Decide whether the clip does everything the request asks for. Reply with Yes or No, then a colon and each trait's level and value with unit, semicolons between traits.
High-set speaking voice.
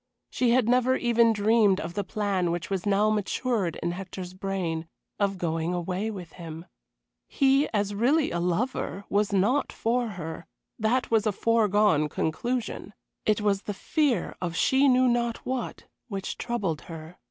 Yes: high, 205 Hz